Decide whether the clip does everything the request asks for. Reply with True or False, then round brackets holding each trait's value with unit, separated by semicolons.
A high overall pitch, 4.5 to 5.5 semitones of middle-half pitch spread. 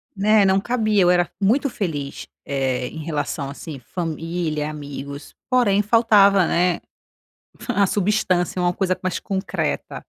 False (180 Hz; 4.9 semitones)